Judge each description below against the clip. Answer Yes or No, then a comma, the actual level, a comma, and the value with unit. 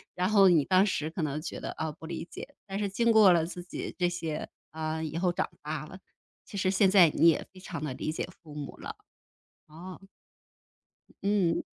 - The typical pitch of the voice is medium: Yes, medium, 175 Hz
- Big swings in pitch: No, average, 3.2 semitones